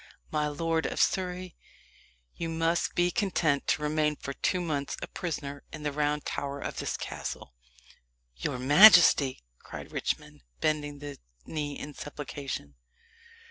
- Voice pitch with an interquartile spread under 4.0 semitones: Yes, narrow, 2.5 semitones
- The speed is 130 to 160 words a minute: Yes, average, 140 wpm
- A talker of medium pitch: Yes, medium, 150 Hz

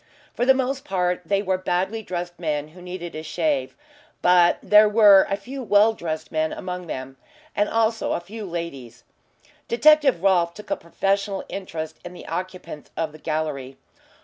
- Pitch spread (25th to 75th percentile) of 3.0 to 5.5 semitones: Yes, average, 4.5 semitones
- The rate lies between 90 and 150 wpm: No, average, 170 wpm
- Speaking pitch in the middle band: Yes, medium, 180 Hz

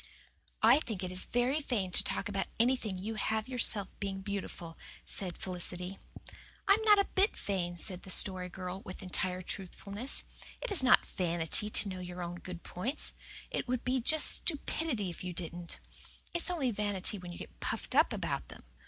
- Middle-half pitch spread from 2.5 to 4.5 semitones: No, average, 5.3 semitones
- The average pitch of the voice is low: No, high, 195 Hz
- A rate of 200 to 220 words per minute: No, average, 185 wpm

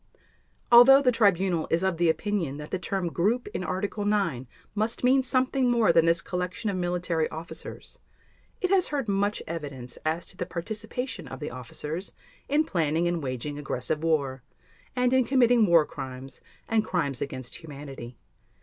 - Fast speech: No, average, 165 wpm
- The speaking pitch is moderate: Yes, medium, 175 Hz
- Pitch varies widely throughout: Yes, wide, 6.6 semitones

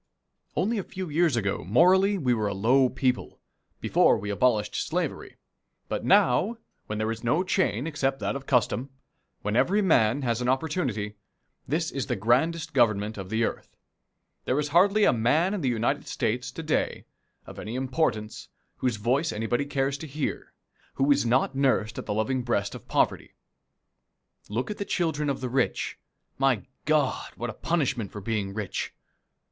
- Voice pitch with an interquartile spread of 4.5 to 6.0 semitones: Yes, wide, 5.5 semitones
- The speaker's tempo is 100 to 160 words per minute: No, average, 175 wpm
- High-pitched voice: No, low, 130 Hz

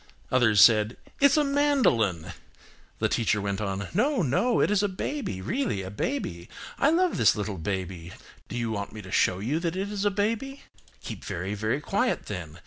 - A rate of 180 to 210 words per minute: Yes, average, 185 wpm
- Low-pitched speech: Yes, low, 120 Hz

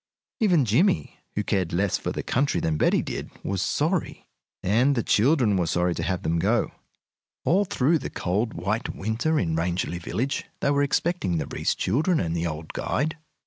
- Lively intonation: Yes, wide, 8.5 semitones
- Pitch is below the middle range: Yes, low, 110 Hz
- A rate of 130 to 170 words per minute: No, average, 185 wpm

